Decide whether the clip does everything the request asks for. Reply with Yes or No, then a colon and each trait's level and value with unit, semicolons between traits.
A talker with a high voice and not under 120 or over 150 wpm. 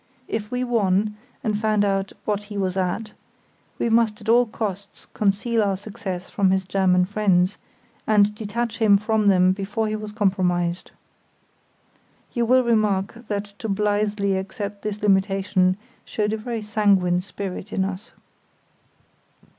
Yes: high, 205 Hz; average, 145 wpm